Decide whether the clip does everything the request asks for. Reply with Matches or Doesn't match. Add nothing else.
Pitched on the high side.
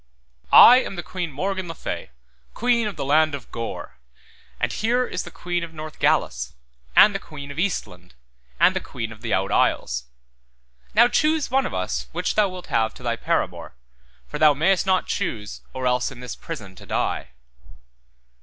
Doesn't match